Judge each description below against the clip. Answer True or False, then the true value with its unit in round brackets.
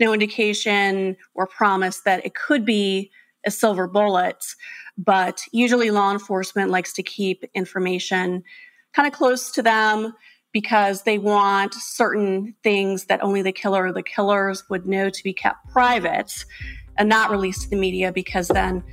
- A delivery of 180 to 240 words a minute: False (160 wpm)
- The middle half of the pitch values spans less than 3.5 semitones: True (2.5 semitones)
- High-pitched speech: True (200 Hz)